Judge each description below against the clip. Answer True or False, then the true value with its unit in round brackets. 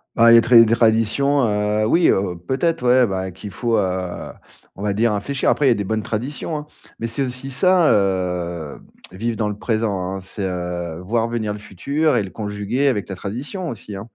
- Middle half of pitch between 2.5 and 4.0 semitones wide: False (4.4 semitones)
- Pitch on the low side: True (110 Hz)